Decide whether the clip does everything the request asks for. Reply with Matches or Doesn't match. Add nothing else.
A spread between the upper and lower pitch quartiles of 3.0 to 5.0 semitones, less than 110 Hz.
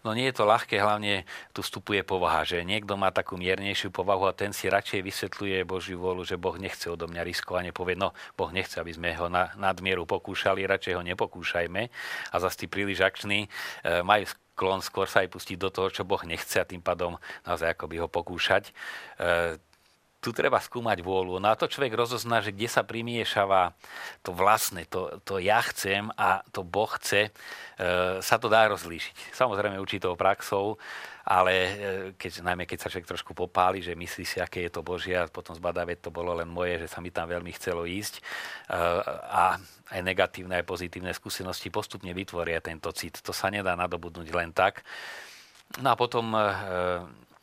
Doesn't match